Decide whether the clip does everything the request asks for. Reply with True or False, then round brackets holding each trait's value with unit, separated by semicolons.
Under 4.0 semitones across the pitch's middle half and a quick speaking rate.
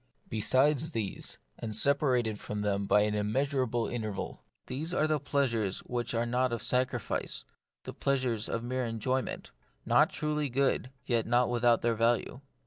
False (2.9 semitones; 155 wpm)